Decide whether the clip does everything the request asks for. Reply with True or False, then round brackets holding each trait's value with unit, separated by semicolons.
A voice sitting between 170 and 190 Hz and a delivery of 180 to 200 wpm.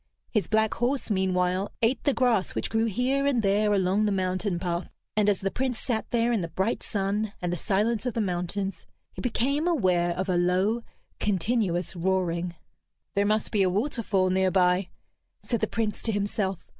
False (200 Hz; 185 wpm)